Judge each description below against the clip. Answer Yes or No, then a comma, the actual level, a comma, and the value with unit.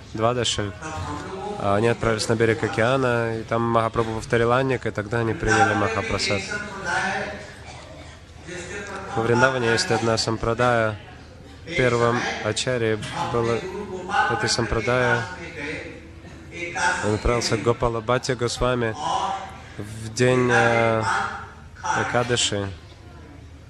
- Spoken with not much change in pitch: Yes, narrow, 1.8 semitones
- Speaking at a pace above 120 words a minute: No, slow, 90 wpm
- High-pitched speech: No, low, 115 Hz